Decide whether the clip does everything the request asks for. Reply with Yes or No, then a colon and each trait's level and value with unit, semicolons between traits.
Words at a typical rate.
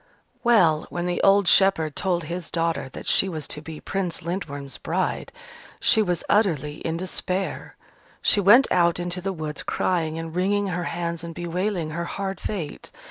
Yes: average, 170 wpm